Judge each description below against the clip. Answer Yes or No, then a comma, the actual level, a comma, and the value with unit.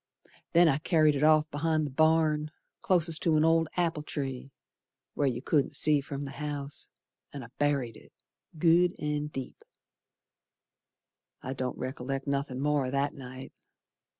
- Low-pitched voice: No, medium, 145 Hz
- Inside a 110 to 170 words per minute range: Yes, average, 150 wpm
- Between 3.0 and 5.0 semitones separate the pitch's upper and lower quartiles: No, narrow, 2.5 semitones